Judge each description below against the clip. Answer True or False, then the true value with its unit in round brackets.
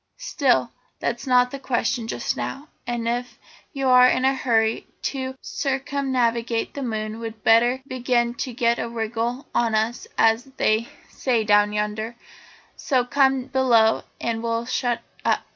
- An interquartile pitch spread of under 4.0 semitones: True (2.5 semitones)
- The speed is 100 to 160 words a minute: True (150 wpm)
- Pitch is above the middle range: True (240 Hz)